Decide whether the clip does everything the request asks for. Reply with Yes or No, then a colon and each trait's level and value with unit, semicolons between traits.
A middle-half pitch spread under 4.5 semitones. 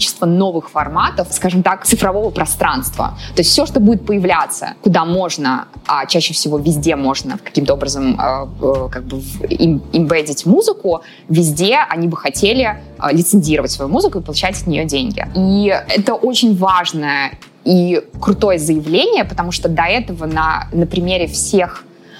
Yes: average, 3.8 semitones